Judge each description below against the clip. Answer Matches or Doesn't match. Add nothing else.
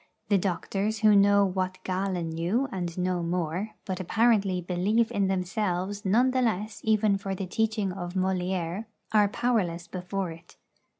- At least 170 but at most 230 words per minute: Doesn't match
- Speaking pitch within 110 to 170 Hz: Doesn't match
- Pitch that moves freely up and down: Doesn't match